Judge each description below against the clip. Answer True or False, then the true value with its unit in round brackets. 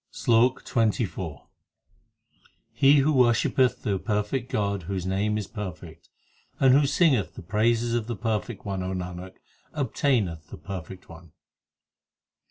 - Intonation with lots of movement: False (4.6 semitones)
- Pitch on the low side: True (105 Hz)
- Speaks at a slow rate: True (130 wpm)